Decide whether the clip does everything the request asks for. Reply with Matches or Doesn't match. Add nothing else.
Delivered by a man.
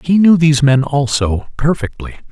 Matches